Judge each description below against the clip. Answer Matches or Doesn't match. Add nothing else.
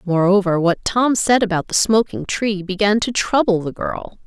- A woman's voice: Matches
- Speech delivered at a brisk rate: Doesn't match